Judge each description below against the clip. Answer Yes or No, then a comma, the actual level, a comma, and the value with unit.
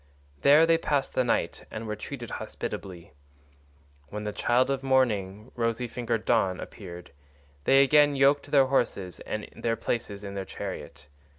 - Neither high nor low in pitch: No, low, 115 Hz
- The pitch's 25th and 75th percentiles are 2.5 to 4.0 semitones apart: No, average, 4.8 semitones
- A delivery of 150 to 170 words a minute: Yes, average, 155 wpm